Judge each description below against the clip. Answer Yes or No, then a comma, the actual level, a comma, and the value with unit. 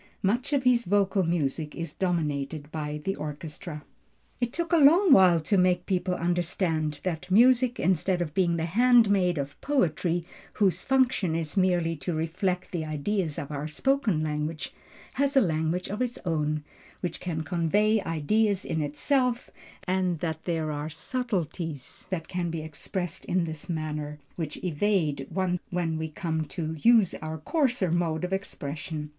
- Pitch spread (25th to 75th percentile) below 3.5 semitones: No, average, 4.1 semitones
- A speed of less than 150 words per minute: No, average, 160 wpm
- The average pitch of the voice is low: No, medium, 175 Hz